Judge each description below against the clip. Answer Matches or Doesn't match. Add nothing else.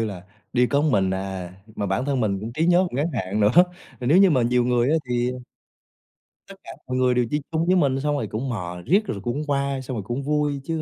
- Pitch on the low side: Matches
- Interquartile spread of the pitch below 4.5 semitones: Doesn't match